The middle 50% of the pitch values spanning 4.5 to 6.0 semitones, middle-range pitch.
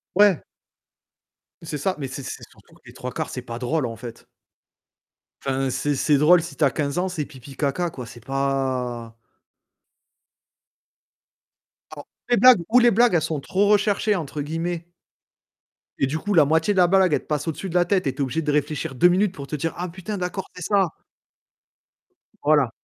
Yes: average, 4.9 semitones; medium, 155 Hz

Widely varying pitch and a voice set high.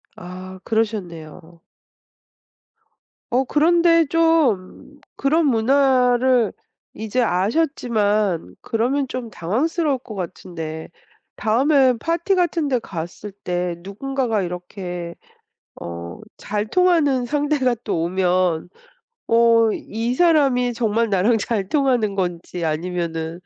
Yes: wide, 7.0 semitones; high, 225 Hz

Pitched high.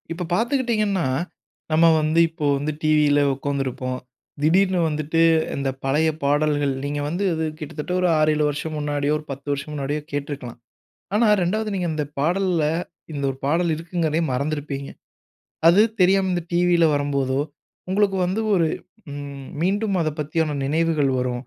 No: medium, 155 Hz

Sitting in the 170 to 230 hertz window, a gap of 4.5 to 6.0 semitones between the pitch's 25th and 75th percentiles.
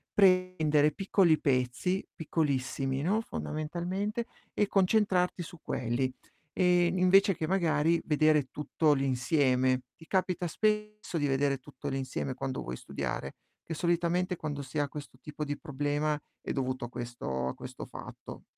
No: medium, 155 Hz; average, 5.1 semitones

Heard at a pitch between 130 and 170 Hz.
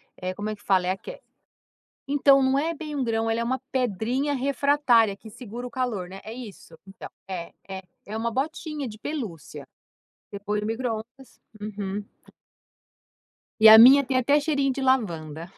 No: high, 235 Hz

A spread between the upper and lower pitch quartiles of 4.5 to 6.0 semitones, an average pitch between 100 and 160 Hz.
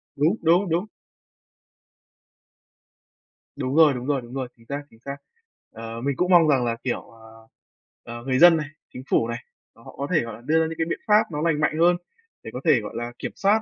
Yes: wide, 5.5 semitones; medium, 140 Hz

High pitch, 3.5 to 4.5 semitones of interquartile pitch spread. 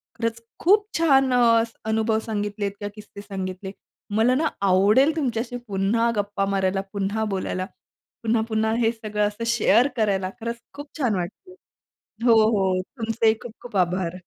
No: high, 220 Hz; average, 3.0 semitones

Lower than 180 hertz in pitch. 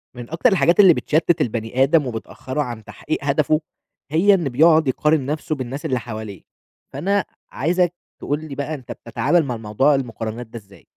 Yes: medium, 140 Hz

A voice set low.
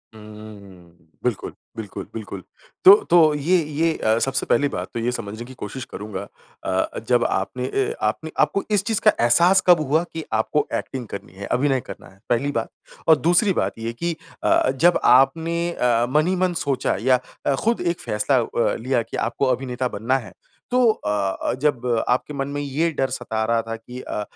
Yes: low, 125 Hz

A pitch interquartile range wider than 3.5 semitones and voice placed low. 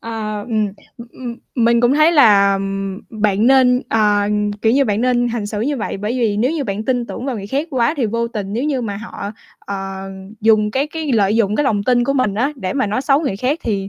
No: average, 3.9 semitones; high, 225 Hz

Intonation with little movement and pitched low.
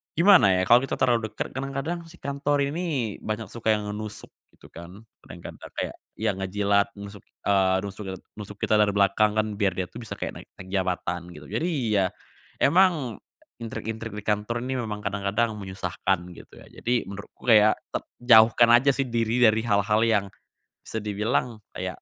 No: average, 3.1 semitones; low, 110 Hz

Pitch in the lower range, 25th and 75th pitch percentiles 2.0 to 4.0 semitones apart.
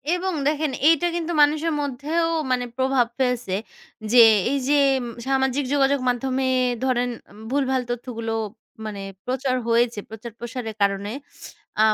No: very high, 260 Hz; average, 3.0 semitones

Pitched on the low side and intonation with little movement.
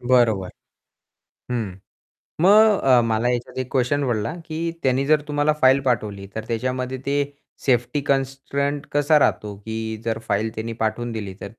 No: low, 125 Hz; average, 4.0 semitones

